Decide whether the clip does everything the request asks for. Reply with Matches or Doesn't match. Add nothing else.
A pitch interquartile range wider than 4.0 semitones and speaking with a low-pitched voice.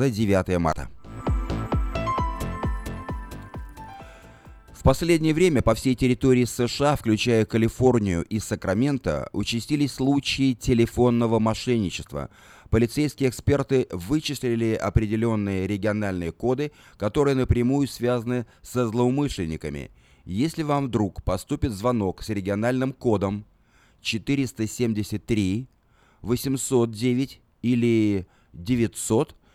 Matches